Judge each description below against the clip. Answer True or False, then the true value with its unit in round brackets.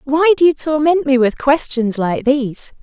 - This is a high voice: True (275 Hz)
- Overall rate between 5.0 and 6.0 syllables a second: False (4.6 syllables/s)